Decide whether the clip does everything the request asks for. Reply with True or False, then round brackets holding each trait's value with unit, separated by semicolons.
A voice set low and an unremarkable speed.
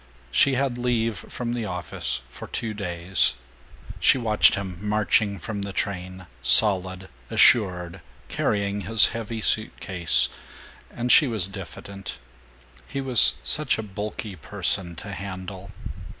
False (100 Hz; 130 wpm)